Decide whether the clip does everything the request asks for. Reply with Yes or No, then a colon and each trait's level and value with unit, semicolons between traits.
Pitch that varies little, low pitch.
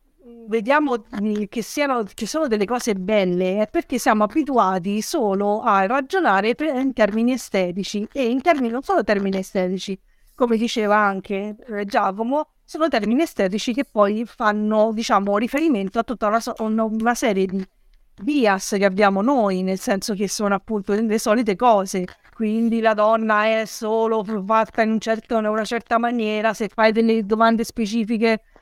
No: narrow, 2.3 semitones; high, 220 Hz